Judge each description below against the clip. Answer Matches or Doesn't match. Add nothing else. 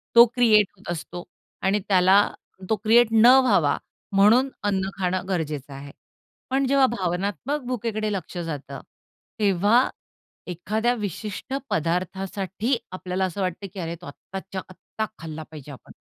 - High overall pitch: Matches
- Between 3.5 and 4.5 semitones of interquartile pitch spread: Matches